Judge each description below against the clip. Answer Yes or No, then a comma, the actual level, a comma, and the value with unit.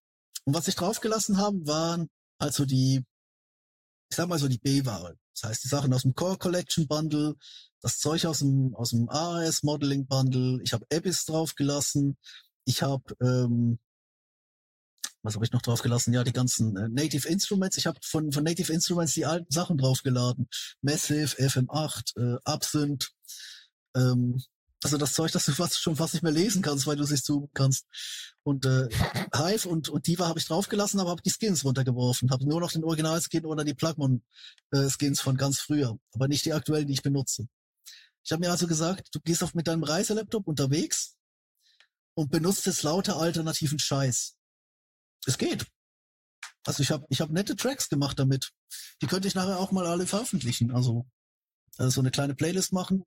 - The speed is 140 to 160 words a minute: No, average, 180 wpm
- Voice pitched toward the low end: No, medium, 150 Hz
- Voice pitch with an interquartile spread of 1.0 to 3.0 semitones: No, average, 4.3 semitones